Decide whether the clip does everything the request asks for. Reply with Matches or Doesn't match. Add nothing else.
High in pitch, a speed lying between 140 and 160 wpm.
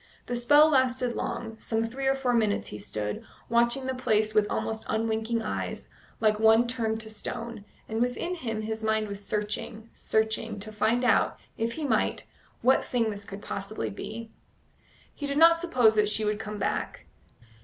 Doesn't match